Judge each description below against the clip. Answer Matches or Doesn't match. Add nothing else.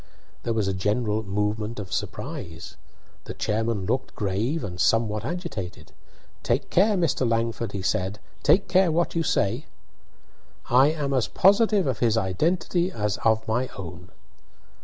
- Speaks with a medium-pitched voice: Doesn't match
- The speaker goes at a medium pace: Matches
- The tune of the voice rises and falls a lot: Matches